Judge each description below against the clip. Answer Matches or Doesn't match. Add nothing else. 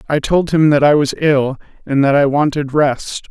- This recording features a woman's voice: Doesn't match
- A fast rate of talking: Matches